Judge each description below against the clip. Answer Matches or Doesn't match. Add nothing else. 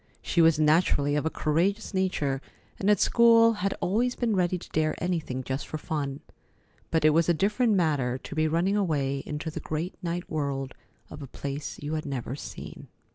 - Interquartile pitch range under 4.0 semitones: Doesn't match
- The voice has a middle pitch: Matches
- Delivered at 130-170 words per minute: Doesn't match